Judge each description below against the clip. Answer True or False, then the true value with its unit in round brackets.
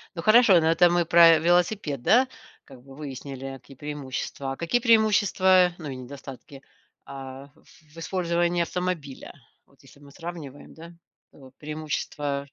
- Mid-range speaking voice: True (155 Hz)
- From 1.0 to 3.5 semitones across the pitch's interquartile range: False (4.2 semitones)